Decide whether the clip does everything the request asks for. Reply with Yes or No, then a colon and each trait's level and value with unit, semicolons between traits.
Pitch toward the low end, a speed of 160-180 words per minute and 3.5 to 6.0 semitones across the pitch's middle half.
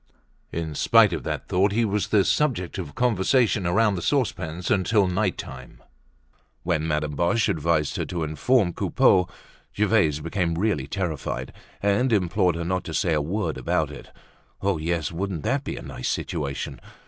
Yes: very low, 90 Hz; average, 165 wpm; average, 4.6 semitones